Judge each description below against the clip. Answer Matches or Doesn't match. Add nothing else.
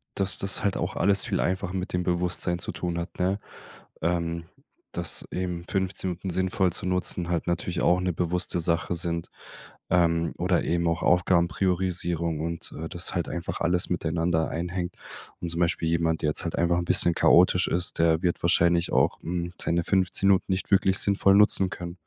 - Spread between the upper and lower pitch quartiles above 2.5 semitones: Doesn't match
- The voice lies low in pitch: Matches